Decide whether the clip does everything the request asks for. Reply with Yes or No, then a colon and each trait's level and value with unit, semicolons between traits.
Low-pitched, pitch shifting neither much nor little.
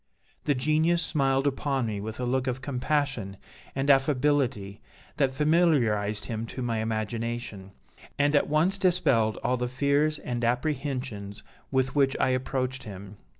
Yes: low, 130 Hz; average, 4.2 semitones